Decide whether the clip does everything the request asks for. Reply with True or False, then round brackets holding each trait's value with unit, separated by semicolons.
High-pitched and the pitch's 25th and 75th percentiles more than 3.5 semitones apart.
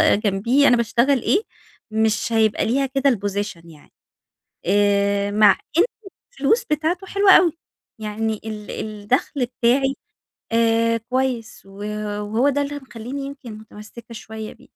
True (230 Hz; 4.3 semitones)